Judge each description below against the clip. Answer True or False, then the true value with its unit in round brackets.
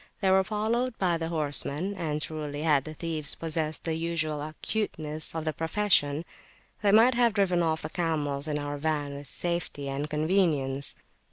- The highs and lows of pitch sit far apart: False (3.3 semitones)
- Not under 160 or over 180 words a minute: True (170 wpm)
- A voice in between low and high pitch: True (160 Hz)